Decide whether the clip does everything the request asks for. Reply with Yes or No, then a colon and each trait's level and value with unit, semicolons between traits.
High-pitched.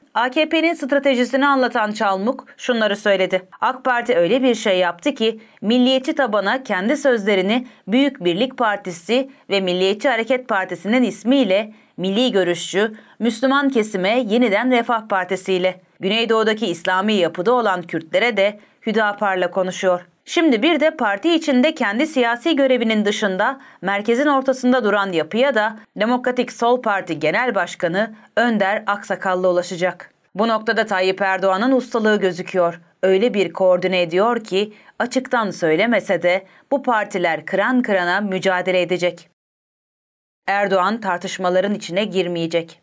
Yes: high, 210 Hz